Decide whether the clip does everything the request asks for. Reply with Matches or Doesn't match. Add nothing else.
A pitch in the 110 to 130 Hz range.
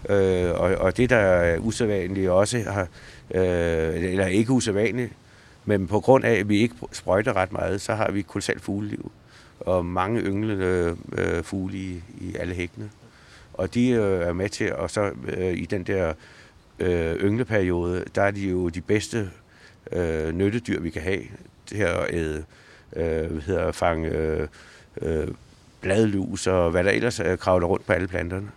Doesn't match